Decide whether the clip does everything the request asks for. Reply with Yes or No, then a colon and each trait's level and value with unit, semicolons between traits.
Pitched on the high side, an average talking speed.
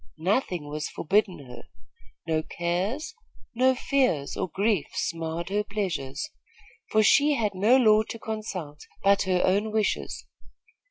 No: high, 200 Hz; slow, 130 wpm